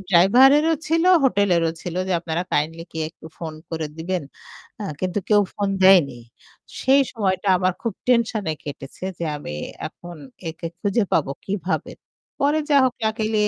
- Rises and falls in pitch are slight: No, average, 5.2 semitones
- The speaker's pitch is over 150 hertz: Yes, medium, 185 Hz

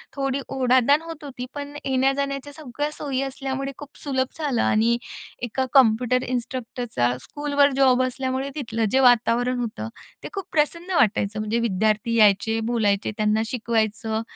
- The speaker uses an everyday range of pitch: Yes, average, 3.7 semitones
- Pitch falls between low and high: No, very high, 255 Hz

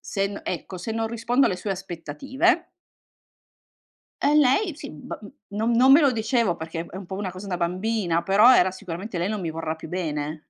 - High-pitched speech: Yes, high, 195 Hz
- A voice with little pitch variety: No, average, 5.0 semitones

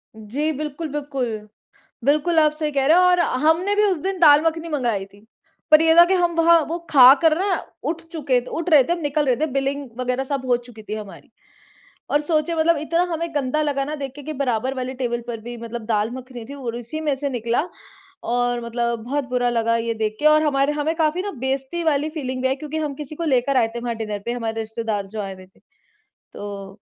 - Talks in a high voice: Yes, very high, 275 Hz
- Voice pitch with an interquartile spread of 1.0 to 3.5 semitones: No, average, 4.6 semitones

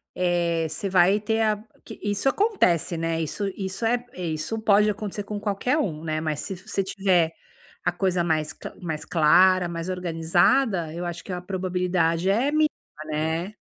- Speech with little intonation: No, average, 3.6 semitones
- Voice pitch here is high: No, medium, 180 Hz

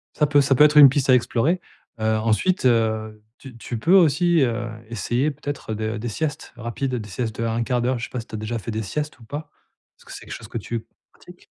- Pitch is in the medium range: No, low, 120 Hz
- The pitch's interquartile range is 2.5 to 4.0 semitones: No, average, 4.4 semitones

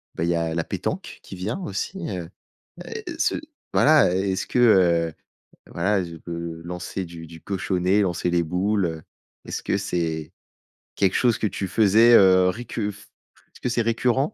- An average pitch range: Yes, average, 3.7 semitones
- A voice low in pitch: Yes, very low, 95 Hz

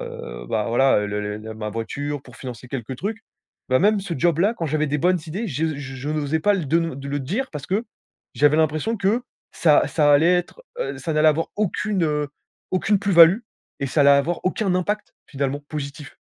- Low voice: No, medium, 155 Hz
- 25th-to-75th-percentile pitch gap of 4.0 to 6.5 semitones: Yes, average, 4.9 semitones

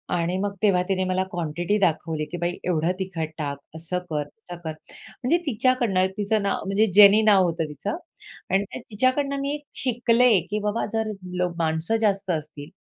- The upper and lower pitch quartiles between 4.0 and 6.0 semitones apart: Yes, average, 4.7 semitones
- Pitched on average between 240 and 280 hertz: No, high, 195 Hz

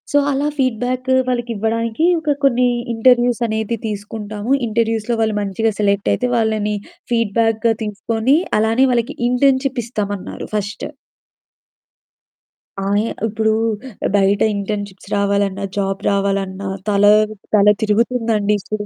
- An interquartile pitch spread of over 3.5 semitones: No, average, 2.7 semitones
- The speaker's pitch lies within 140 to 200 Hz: No, high, 220 Hz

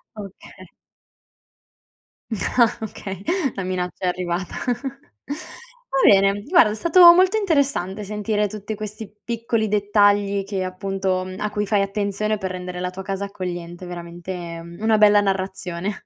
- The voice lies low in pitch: No, high, 200 Hz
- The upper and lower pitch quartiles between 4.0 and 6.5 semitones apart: No, narrow, 2.5 semitones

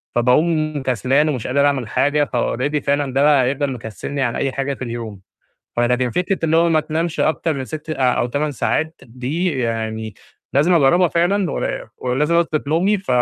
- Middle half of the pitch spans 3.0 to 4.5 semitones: Yes, average, 4.0 semitones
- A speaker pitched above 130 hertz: Yes, medium, 140 Hz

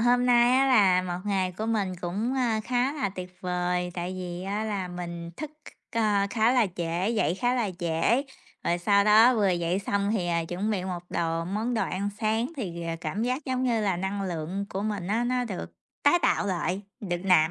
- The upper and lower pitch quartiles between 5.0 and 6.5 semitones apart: No, average, 4.3 semitones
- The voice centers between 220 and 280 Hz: No, high, 200 Hz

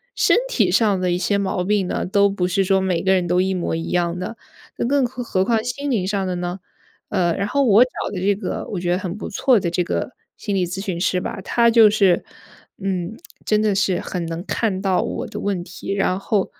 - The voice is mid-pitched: No, high, 195 Hz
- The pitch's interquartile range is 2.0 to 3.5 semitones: Yes, narrow, 2.6 semitones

